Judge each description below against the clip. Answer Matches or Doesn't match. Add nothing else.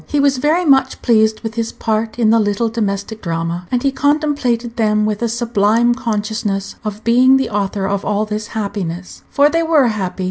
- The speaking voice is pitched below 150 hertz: Doesn't match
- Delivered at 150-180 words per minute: Doesn't match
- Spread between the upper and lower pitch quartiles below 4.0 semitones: Matches